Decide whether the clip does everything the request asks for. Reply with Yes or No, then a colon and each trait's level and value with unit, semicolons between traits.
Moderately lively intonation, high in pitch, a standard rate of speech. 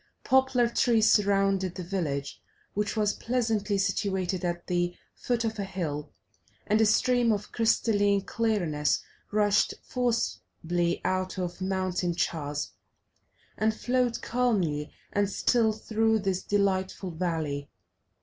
No: average, 3.9 semitones; high, 200 Hz; slow, 120 wpm